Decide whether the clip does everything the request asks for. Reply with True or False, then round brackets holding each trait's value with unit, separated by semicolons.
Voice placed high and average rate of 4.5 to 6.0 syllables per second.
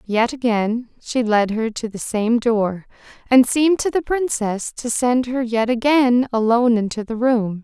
False (235 Hz; 4.3 syllables/s)